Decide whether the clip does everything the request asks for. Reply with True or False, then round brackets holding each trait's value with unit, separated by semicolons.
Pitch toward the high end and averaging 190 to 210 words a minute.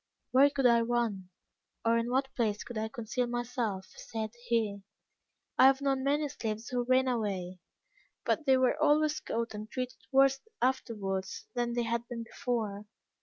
False (240 Hz; 165 wpm)